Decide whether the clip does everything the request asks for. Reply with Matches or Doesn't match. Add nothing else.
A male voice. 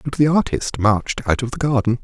Matches